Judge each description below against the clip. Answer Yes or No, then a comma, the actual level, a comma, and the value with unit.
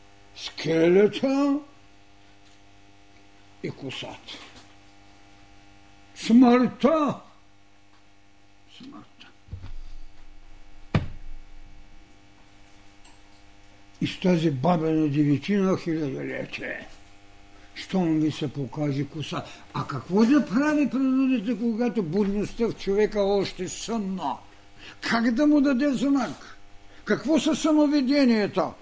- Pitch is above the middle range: No, low, 135 Hz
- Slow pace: Yes, slow, 75 wpm